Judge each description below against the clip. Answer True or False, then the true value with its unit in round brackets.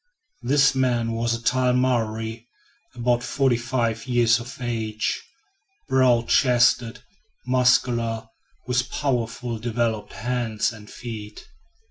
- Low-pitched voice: True (120 Hz)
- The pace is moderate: False (105 wpm)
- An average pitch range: False (1.7 semitones)